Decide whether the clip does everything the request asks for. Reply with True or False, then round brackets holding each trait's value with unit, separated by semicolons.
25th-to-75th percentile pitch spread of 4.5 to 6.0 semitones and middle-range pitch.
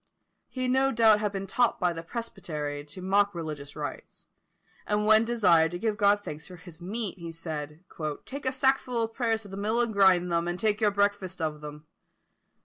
False (4.9 semitones; 200 Hz)